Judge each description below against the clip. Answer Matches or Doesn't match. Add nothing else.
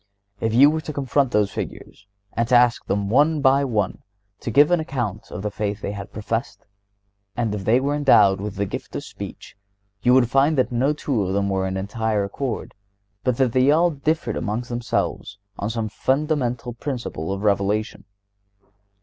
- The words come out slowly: Doesn't match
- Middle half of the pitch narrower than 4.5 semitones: Doesn't match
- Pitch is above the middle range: Doesn't match